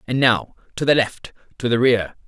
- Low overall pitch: Yes, low, 120 Hz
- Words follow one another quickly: No, average, 185 wpm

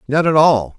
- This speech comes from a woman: No, male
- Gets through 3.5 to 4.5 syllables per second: No, 4.8 syllables/s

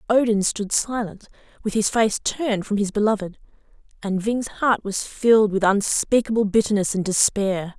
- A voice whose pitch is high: Yes, high, 210 Hz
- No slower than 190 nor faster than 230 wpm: No, average, 160 wpm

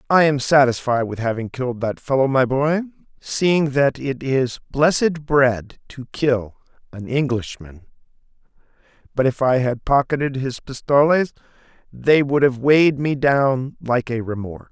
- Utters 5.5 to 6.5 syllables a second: No, 4.4 syllables/s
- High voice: No, low, 135 Hz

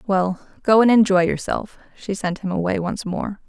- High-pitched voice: Yes, high, 195 Hz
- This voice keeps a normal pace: Yes, average, 190 wpm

